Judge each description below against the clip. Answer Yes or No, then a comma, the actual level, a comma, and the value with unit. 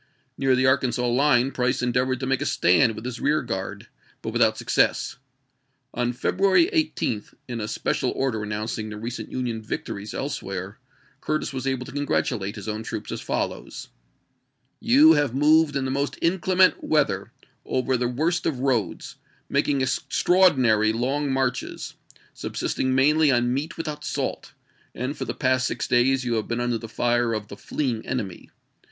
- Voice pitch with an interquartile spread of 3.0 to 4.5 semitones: Yes, average, 3.4 semitones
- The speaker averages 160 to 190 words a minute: Yes, average, 170 wpm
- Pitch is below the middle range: Yes, low, 130 Hz